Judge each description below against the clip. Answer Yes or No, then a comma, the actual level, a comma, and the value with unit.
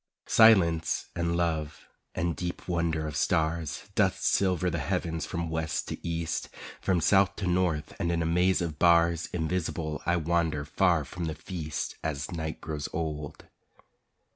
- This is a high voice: No, very low, 85 Hz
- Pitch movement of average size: No, narrow, 1.8 semitones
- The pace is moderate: Yes, average, 155 wpm